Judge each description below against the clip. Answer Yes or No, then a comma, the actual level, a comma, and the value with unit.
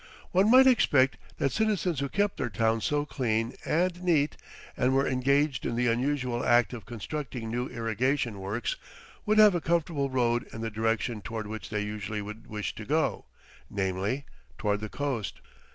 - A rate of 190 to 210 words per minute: No, average, 170 wpm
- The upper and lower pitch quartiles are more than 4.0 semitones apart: Yes, average, 4.8 semitones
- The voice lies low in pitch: Yes, low, 125 Hz